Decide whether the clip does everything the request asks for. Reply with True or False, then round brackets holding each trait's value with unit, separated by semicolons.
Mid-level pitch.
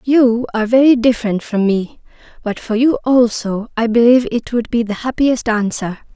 False (235 Hz)